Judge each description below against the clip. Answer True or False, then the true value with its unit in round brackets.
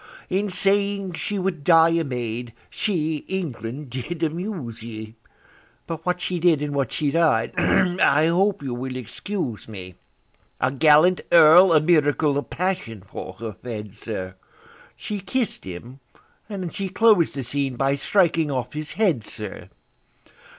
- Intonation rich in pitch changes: True (6.6 semitones)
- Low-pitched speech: False (155 Hz)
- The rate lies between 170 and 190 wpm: False (145 wpm)